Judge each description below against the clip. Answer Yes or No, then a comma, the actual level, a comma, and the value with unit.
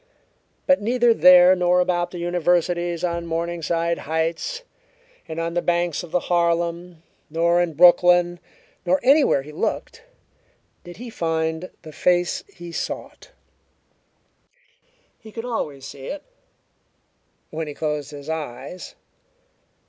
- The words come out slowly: Yes, slow, 125 wpm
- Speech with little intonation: Yes, narrow, 1.7 semitones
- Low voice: No, medium, 175 Hz